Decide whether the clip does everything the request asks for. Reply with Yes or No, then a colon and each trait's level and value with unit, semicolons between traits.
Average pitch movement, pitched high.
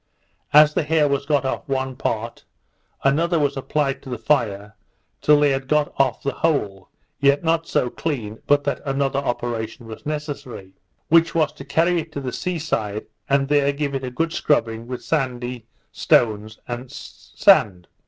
No: average, 3.8 semitones; low, 135 Hz